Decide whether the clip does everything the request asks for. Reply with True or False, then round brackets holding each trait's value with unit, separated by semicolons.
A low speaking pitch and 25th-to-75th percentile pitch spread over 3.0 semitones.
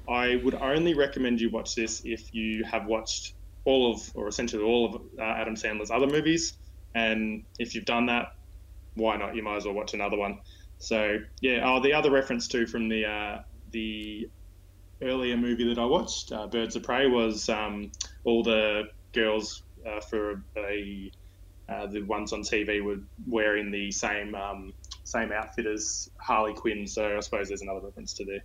False (105 Hz; 2.6 semitones)